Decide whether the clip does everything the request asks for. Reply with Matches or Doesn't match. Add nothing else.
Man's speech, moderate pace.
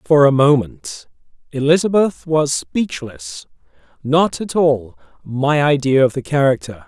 Doesn't match